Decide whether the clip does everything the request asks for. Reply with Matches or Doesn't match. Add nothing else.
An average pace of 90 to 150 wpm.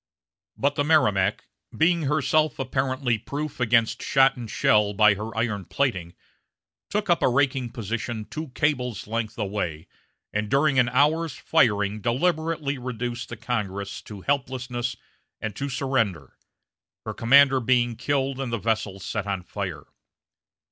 Matches